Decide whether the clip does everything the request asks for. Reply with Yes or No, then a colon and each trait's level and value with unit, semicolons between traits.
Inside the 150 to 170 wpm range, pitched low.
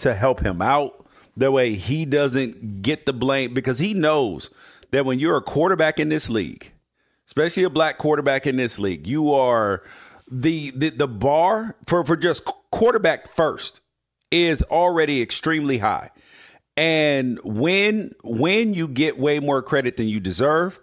No: average, 160 wpm; medium, 145 Hz